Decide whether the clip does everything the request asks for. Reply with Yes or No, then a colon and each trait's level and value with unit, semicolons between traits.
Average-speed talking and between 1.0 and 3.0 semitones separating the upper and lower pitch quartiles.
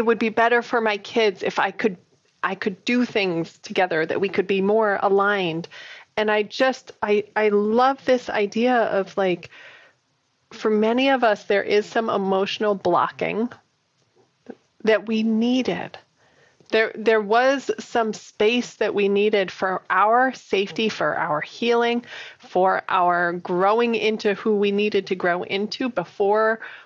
Yes: average, 150 wpm; narrow, 2.5 semitones